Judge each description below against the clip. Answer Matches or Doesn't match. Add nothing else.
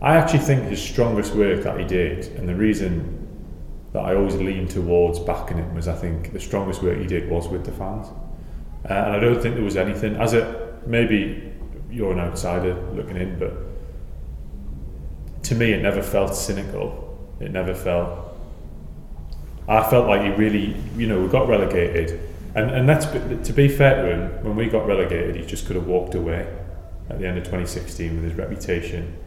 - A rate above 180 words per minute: Matches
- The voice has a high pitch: Doesn't match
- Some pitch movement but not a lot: Matches